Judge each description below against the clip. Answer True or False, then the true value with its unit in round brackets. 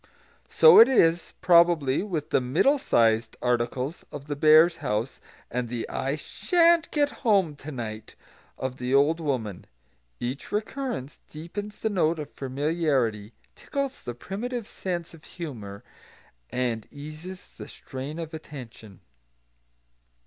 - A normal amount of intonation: False (6.1 semitones)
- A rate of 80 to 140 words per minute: True (135 wpm)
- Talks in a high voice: False (150 Hz)